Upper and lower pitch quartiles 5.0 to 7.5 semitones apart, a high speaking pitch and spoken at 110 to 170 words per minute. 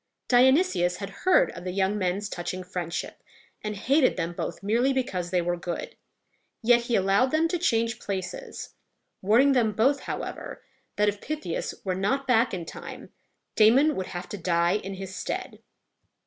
Yes: wide, 5.6 semitones; high, 205 Hz; average, 165 wpm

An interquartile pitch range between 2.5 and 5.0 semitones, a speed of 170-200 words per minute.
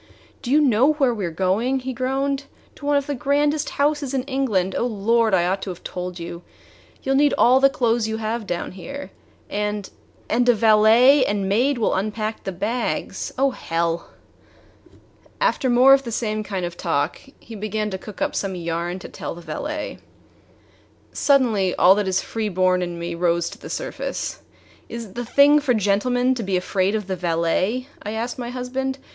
No: wide, 5.6 semitones; average, 195 wpm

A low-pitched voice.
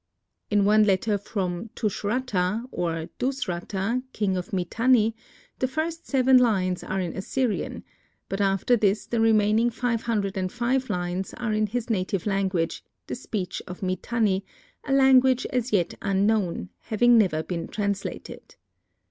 No: high, 210 Hz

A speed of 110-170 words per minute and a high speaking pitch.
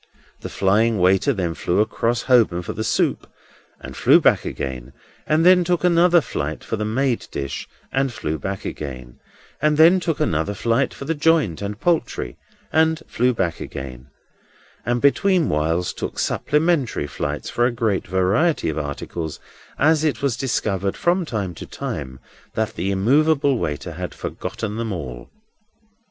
No: average, 160 wpm; low, 110 Hz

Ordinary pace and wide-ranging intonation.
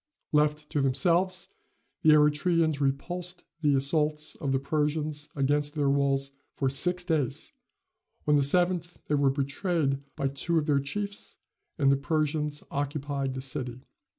No: average, 145 wpm; average, 2.7 semitones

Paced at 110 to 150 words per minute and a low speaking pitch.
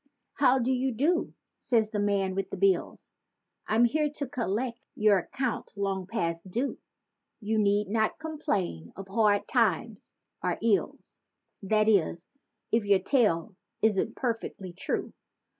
No: average, 140 wpm; high, 215 Hz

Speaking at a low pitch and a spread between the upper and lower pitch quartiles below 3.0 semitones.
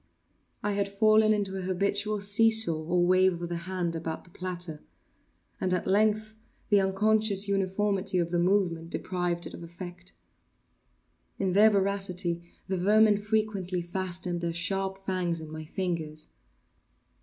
No: medium, 185 Hz; narrow, 2.6 semitones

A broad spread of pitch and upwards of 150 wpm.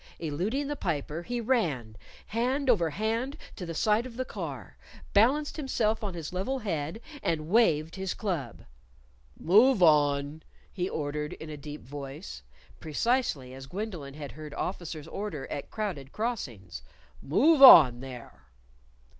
No: wide, 7.6 semitones; average, 140 wpm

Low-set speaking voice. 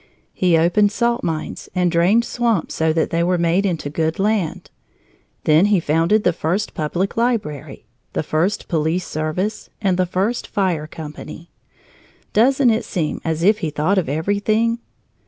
No: medium, 180 Hz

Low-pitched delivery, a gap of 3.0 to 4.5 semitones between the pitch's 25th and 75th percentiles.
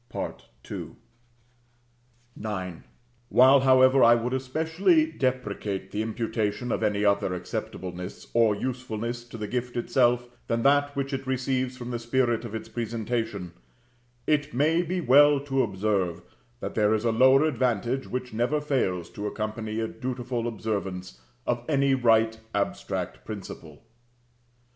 Yes: low, 120 Hz; average, 3.5 semitones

